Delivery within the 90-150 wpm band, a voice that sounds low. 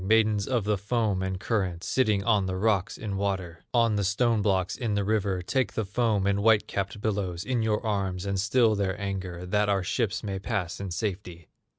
No: fast, 205 wpm; low, 100 Hz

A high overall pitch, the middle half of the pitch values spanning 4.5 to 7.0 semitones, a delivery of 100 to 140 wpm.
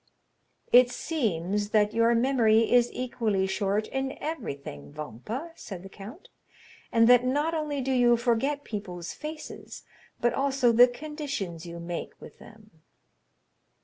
Yes: high, 235 Hz; average, 5.2 semitones; slow, 135 wpm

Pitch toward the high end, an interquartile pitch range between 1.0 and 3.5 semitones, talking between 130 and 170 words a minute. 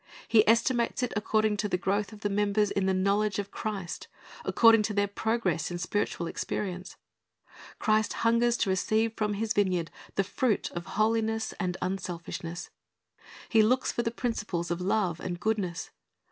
Yes: high, 205 Hz; average, 3.1 semitones; average, 160 wpm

